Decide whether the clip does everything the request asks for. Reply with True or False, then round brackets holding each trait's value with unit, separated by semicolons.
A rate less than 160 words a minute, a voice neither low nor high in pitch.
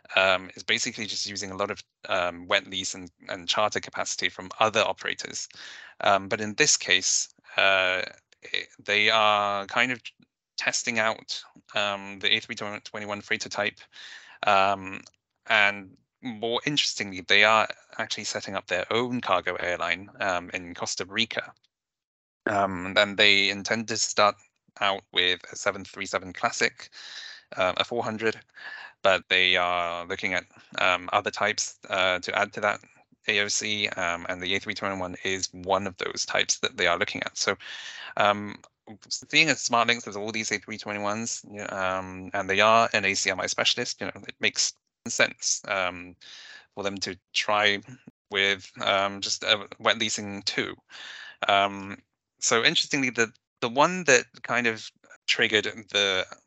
False (150 wpm; 100 Hz)